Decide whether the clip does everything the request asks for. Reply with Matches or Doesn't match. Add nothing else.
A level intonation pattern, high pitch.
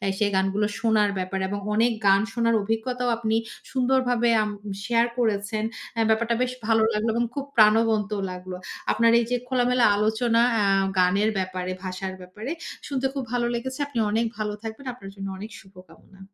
Doesn't match